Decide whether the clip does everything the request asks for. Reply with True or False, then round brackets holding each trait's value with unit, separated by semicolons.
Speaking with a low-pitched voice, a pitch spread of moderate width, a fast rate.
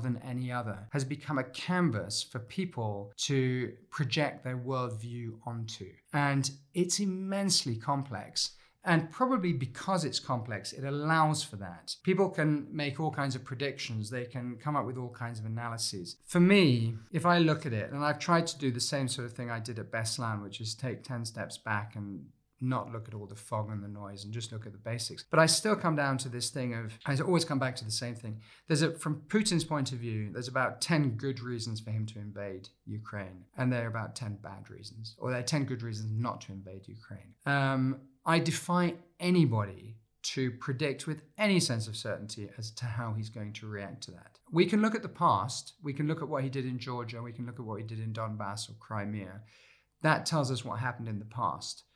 True (125 Hz; 4.9 semitones; 220 wpm)